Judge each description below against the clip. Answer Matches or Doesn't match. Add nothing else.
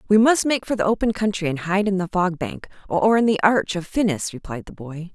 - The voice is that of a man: Doesn't match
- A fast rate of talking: Matches